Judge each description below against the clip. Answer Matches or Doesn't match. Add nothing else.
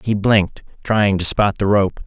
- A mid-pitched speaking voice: Doesn't match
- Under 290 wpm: Matches